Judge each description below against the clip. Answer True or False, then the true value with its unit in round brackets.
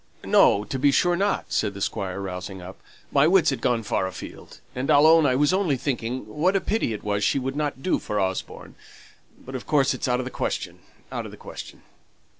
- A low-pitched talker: True (130 Hz)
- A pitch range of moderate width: False (6.6 semitones)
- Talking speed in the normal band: False (220 wpm)